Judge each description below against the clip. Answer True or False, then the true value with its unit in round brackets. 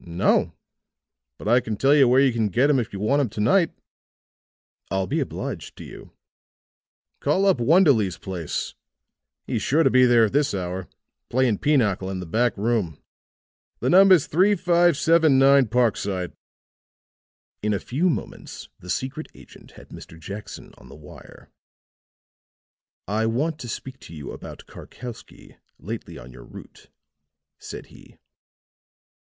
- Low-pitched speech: True (120 Hz)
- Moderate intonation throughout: False (6.4 semitones)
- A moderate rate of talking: True (150 wpm)